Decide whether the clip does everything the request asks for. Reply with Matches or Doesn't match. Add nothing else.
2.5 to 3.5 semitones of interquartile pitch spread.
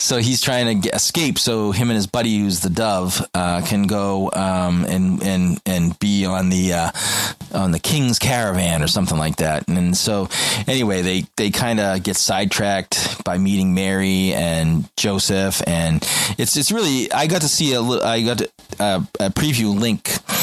Doesn't match